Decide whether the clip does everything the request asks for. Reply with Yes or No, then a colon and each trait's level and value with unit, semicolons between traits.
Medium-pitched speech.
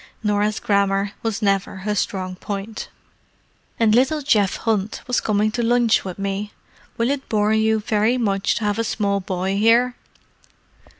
No: high, 210 Hz